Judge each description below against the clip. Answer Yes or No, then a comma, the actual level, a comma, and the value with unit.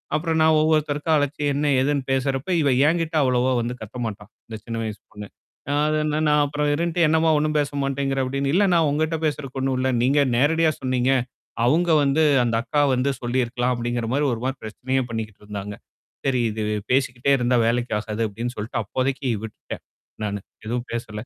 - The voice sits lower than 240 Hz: Yes, low, 135 Hz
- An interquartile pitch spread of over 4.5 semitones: No, average, 3.8 semitones